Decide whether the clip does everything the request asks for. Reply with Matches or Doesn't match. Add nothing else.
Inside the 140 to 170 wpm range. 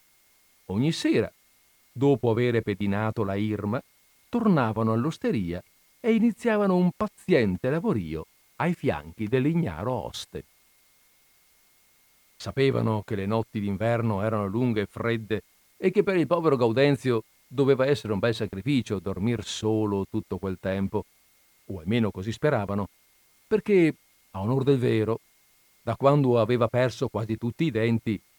Doesn't match